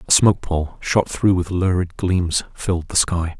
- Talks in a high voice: No, very low, 90 Hz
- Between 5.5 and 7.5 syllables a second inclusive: No, 4.5 syllables/s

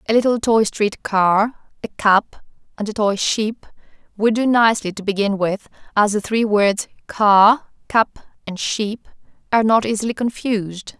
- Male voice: No, female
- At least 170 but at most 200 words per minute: No, average, 160 wpm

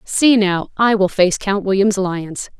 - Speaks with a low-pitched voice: No, high, 195 Hz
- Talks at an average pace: Yes, average, 185 wpm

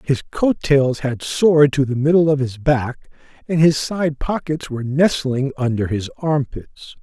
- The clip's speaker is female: No, male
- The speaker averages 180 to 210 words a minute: No, average, 170 wpm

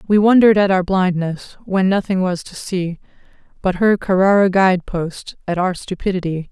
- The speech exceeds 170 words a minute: No, average, 165 wpm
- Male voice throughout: No, female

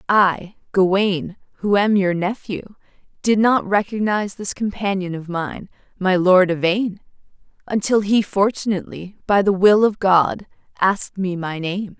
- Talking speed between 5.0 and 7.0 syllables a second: No, 4.4 syllables/s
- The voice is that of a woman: Yes, female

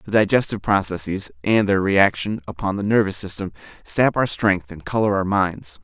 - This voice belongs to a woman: No, male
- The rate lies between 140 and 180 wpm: Yes, average, 175 wpm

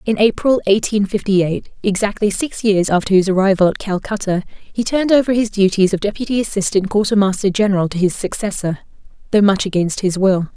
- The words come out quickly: No, average, 170 wpm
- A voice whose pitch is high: Yes, high, 200 Hz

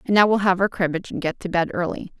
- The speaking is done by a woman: Yes, female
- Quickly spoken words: Yes, fast, 300 wpm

